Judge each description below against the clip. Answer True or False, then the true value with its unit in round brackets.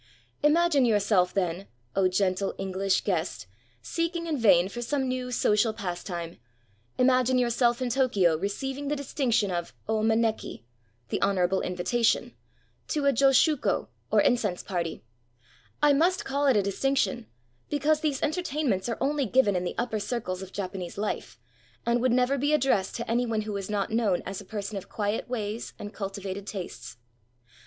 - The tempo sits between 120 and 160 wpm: False (170 wpm)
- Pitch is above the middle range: True (220 Hz)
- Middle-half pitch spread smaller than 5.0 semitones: False (5.5 semitones)